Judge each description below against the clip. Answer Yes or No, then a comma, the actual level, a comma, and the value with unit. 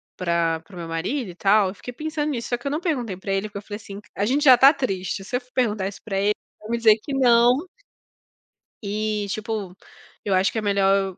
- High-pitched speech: Yes, high, 210 Hz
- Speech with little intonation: No, average, 4.1 semitones